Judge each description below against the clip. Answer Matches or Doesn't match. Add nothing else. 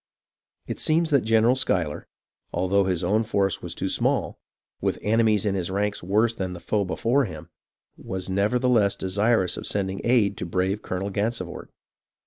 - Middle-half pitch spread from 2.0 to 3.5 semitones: Matches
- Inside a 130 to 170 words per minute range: Matches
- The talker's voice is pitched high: Doesn't match